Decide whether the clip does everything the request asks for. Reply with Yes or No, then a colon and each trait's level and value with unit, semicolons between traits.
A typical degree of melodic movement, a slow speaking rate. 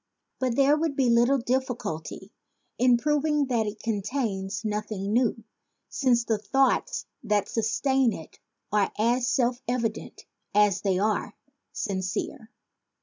Yes: average, 3.8 semitones; slow, 130 wpm